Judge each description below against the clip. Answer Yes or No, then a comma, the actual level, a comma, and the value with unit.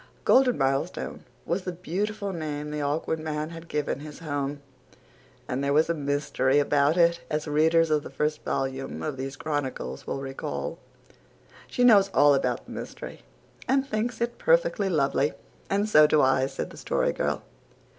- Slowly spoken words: No, average, 165 wpm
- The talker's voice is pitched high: No, medium, 150 Hz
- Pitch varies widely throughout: No, average, 4.3 semitones